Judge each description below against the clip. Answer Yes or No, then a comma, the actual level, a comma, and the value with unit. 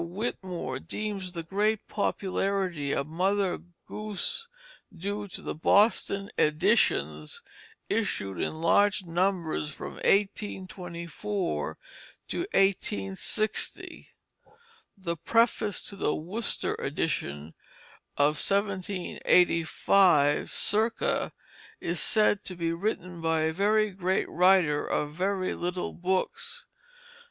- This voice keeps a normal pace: No, slow, 95 wpm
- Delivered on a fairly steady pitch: No, average, 3.6 semitones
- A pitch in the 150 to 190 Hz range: Yes, medium, 185 Hz